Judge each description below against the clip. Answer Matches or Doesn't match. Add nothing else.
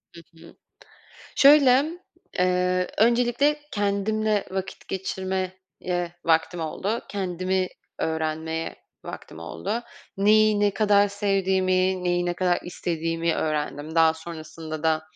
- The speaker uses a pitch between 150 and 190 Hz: Matches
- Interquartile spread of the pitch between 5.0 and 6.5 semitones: Doesn't match